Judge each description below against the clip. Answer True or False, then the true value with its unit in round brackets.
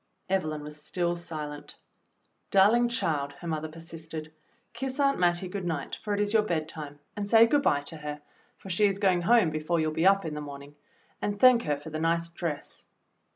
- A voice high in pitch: False (170 Hz)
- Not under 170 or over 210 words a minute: True (200 wpm)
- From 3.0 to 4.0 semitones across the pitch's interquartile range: False (4.7 semitones)